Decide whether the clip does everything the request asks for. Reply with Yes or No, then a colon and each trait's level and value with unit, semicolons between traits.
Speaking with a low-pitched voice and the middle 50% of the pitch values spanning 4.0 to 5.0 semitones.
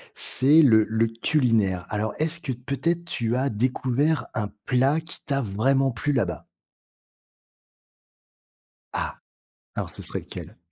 Yes: low, 130 Hz; average, 4.5 semitones